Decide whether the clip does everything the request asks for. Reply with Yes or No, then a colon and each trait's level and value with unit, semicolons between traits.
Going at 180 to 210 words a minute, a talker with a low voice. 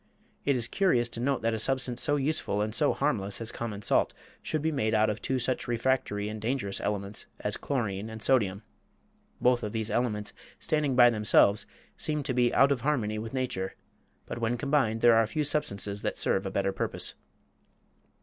Yes: average, 190 wpm; low, 115 Hz